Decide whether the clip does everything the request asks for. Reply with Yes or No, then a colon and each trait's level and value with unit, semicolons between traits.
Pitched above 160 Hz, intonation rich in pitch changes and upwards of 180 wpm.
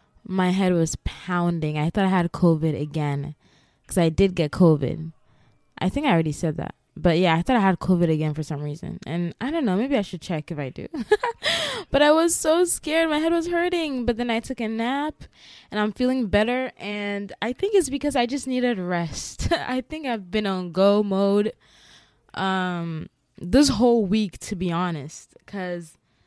Yes: high, 190 Hz; wide, 7.1 semitones; average, 195 wpm